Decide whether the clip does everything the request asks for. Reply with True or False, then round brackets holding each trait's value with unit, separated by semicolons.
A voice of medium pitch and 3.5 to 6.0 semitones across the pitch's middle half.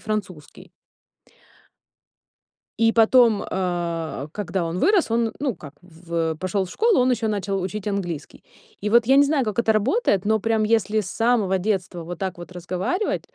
False (200 Hz; 4.2 semitones)